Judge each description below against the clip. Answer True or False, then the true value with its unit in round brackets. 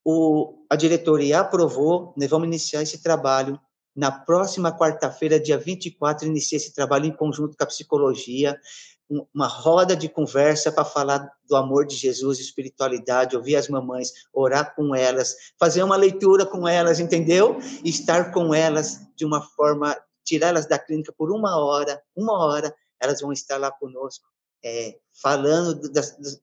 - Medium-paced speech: True (165 wpm)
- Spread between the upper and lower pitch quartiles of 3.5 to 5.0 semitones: False (2.9 semitones)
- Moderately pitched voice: True (150 Hz)